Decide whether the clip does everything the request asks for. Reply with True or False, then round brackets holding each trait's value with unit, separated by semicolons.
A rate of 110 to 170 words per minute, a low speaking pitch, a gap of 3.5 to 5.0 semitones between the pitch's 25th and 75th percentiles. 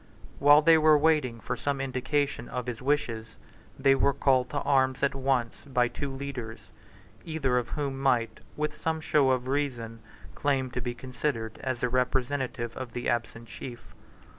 False (165 wpm; 130 Hz; 2.7 semitones)